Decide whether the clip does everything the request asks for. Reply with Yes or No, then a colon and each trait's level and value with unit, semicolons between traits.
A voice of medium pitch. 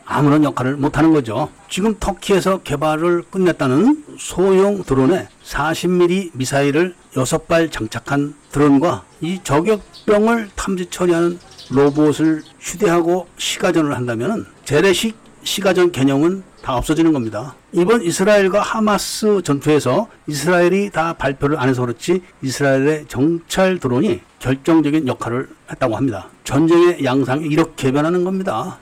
Yes: medium, 160 Hz